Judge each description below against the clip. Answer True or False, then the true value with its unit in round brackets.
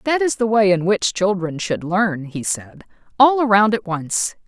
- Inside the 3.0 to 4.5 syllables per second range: True (4.3 syllables/s)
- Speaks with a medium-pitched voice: False (200 Hz)